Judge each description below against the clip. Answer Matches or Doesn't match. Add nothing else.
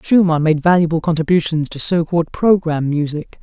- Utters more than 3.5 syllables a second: Matches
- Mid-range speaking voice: Matches